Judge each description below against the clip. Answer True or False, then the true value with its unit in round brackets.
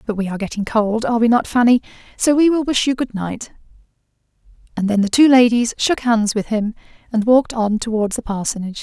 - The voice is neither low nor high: False (230 Hz)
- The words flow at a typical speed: True (195 wpm)